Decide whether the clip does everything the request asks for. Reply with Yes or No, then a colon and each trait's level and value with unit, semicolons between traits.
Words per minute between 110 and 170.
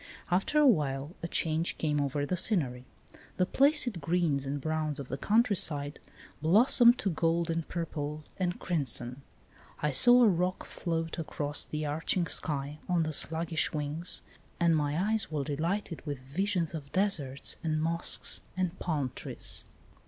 Yes: average, 150 wpm